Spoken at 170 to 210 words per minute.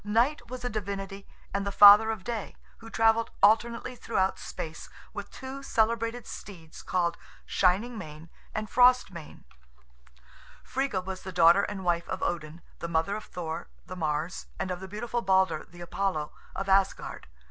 No: average, 160 wpm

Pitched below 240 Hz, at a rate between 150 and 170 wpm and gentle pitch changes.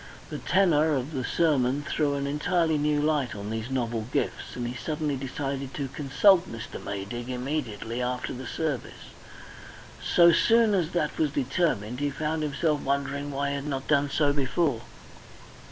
No: medium, 140 Hz; average, 165 wpm; average, 3.3 semitones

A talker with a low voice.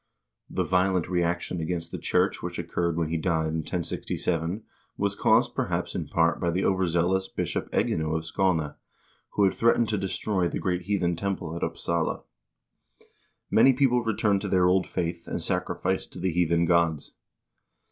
Yes: very low, 90 Hz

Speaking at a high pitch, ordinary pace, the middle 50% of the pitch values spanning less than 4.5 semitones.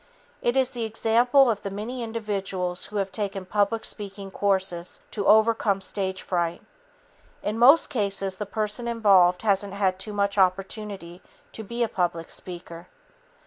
Yes: high, 200 Hz; average, 150 wpm; average, 2.7 semitones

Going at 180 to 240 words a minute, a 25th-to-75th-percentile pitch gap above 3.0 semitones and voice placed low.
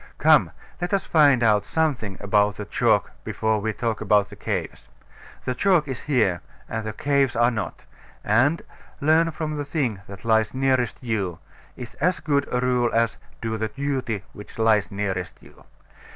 No: average, 170 wpm; average, 5.0 semitones; low, 115 Hz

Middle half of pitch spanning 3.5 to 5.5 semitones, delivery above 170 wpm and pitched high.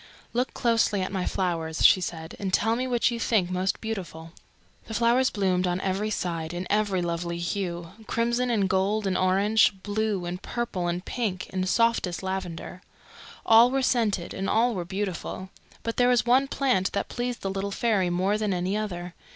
Yes: average, 3.9 semitones; average, 185 wpm; high, 195 Hz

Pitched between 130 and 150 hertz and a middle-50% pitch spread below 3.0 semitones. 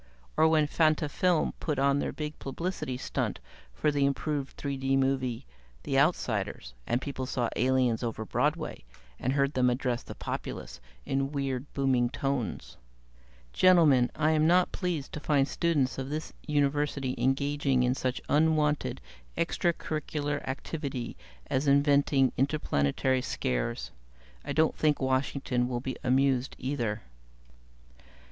Yes: medium, 140 Hz; narrow, 2.6 semitones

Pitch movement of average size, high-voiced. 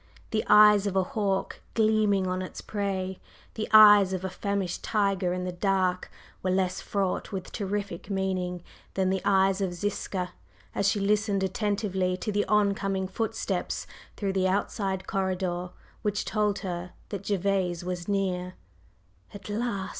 No: narrow, 1.8 semitones; high, 195 Hz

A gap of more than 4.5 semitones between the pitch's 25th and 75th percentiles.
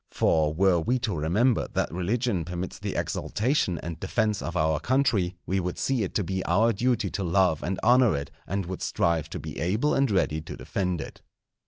Yes: average, 5.0 semitones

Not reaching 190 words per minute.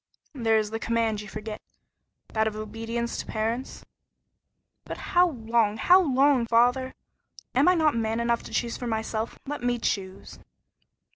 Yes: average, 155 wpm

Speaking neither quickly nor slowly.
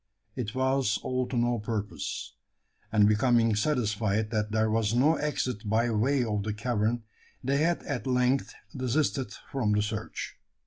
Yes: average, 150 wpm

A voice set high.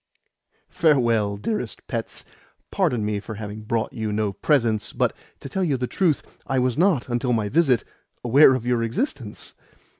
No: low, 120 Hz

